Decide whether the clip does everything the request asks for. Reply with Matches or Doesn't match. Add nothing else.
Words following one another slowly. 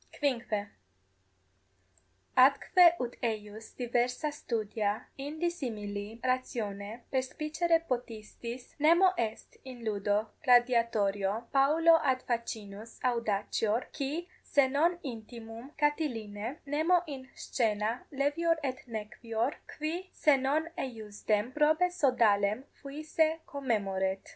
Matches